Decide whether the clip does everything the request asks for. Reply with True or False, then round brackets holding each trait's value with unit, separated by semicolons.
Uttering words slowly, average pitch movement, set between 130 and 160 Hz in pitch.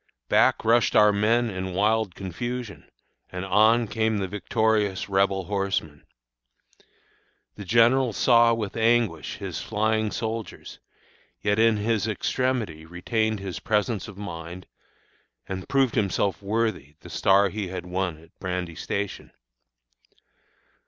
False (125 wpm; 3.1 semitones; 105 Hz)